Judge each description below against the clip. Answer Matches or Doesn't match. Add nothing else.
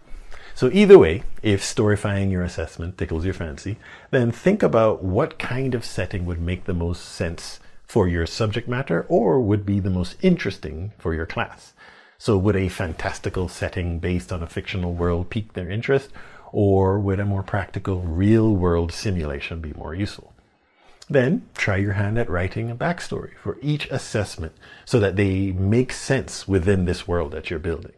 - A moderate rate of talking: Matches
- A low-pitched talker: Matches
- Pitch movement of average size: Matches